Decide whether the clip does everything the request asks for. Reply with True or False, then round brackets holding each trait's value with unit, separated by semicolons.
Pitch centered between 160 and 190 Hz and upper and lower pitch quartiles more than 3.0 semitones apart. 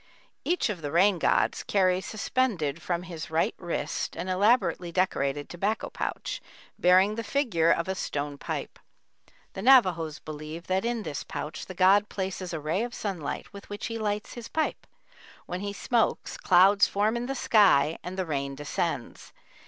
True (185 Hz; 4.2 semitones)